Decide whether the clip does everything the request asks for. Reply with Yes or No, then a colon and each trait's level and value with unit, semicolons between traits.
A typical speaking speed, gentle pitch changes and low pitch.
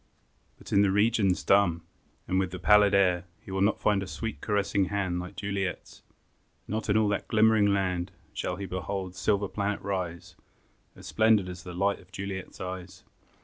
Yes: average, 185 wpm; narrow, 1.8 semitones; low, 100 Hz